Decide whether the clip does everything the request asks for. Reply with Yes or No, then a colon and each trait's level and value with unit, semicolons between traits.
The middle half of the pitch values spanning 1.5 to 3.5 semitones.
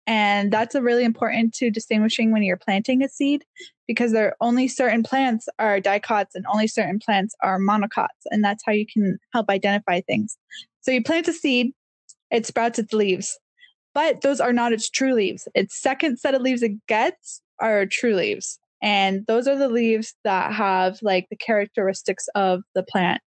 No: average, 4.2 semitones